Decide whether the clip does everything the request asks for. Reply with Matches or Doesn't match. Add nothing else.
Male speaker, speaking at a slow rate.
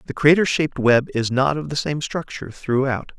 Doesn't match